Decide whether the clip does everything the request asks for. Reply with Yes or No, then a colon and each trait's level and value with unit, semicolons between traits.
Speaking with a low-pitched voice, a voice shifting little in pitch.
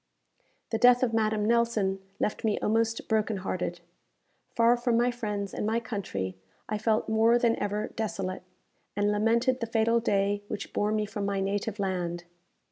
No: high, 215 Hz; narrow, 2.3 semitones